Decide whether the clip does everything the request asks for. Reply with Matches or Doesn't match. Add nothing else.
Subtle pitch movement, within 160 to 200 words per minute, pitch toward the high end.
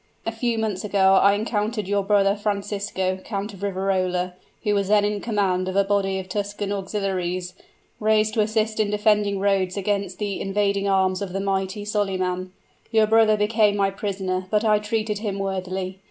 Matches